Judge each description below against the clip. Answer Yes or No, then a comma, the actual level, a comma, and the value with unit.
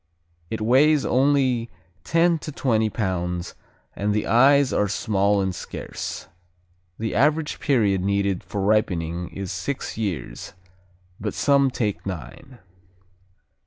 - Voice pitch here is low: Yes, low, 110 Hz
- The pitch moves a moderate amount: No, wide, 5.7 semitones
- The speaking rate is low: Yes, slow, 120 wpm